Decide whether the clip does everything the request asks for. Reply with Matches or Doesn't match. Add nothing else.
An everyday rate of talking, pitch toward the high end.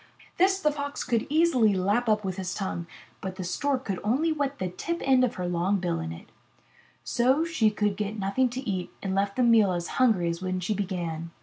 Doesn't match